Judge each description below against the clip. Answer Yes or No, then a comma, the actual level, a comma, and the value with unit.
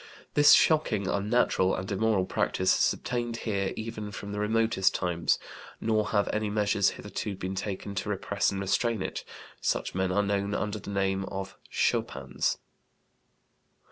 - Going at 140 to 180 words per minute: Yes, average, 150 wpm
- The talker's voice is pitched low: Yes, low, 100 Hz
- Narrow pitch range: Yes, narrow, 2.0 semitones